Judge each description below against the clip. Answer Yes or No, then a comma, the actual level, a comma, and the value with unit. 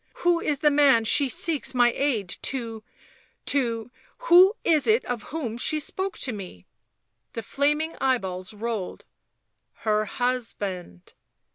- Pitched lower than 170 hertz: No, high, 245 Hz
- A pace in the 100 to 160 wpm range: Yes, average, 140 wpm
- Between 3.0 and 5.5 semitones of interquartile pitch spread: Yes, average, 5.1 semitones